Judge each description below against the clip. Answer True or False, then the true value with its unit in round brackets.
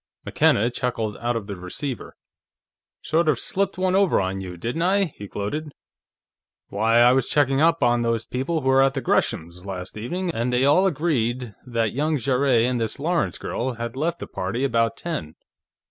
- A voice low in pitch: True (125 Hz)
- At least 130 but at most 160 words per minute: False (180 wpm)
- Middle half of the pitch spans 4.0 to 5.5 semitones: True (5.2 semitones)